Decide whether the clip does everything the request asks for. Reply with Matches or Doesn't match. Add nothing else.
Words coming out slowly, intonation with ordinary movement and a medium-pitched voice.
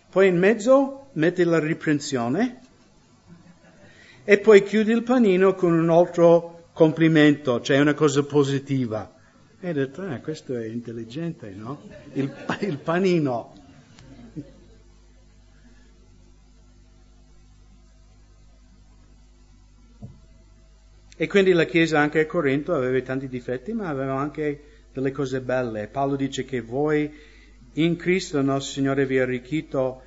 Matches